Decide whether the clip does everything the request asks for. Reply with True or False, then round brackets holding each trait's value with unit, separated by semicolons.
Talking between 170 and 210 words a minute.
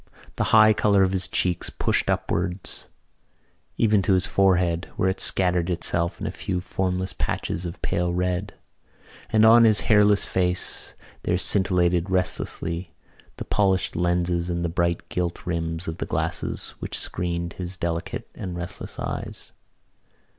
False (145 wpm)